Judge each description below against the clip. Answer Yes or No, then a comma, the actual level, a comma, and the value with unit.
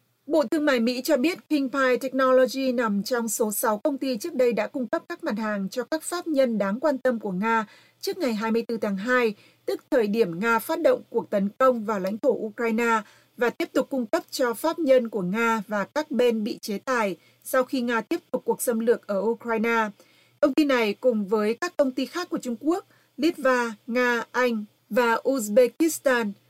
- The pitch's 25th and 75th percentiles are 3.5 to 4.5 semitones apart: Yes, average, 3.9 semitones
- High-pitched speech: Yes, high, 245 Hz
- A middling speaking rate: Yes, average, 210 wpm